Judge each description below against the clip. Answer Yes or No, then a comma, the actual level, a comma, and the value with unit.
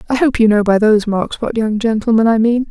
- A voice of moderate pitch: No, high, 225 Hz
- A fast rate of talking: Yes, fast, 265 wpm